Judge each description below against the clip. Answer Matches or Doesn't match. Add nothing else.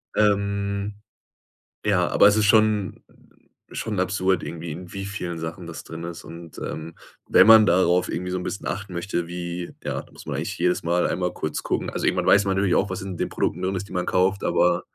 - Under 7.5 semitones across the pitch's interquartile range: Matches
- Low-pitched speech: Matches